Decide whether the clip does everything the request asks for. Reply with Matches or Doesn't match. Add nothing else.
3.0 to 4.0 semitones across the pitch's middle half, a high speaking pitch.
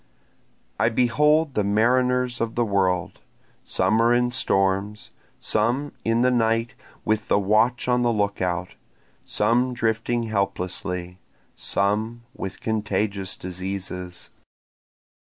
Doesn't match